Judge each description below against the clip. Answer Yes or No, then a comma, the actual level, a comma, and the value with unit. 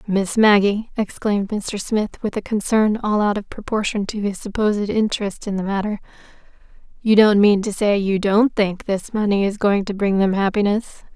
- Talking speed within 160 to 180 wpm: No, average, 190 wpm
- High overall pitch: Yes, high, 205 Hz